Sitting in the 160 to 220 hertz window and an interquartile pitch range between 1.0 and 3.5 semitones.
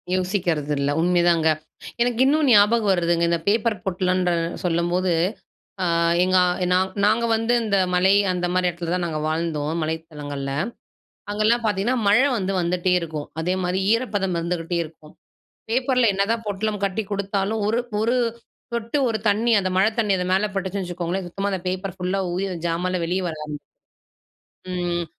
Yes: medium, 185 Hz; average, 3.2 semitones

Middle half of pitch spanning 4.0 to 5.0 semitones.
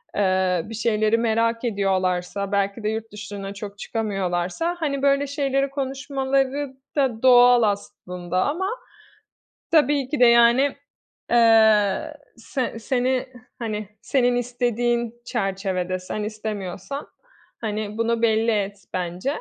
Yes: average, 4.4 semitones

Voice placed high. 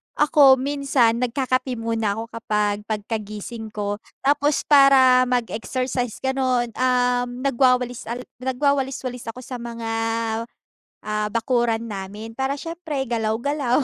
Yes: high, 245 Hz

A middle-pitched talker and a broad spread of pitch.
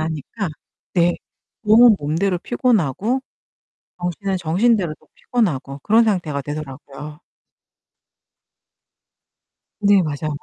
Yes: medium, 175 Hz; wide, 5.8 semitones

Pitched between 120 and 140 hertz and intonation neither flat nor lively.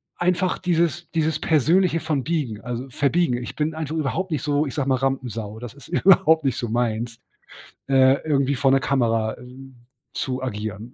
Yes: low, 135 Hz; average, 4.6 semitones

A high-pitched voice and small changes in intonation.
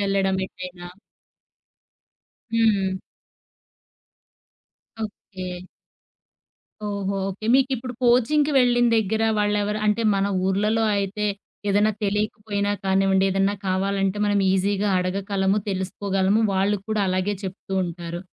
Yes: high, 200 Hz; narrow, 1.7 semitones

